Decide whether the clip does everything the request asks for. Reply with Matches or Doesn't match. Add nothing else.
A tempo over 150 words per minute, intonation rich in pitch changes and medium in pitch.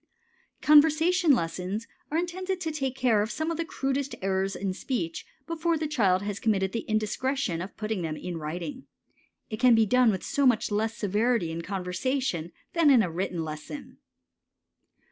Doesn't match